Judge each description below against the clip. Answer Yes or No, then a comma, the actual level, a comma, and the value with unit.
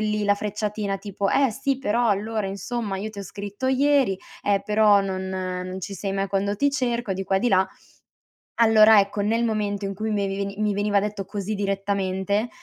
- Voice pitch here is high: Yes, high, 205 Hz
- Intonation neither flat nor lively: No, narrow, 1.8 semitones